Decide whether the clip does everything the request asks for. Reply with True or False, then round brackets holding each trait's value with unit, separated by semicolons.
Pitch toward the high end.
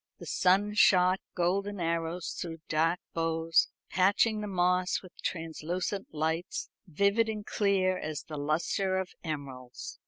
False (180 Hz)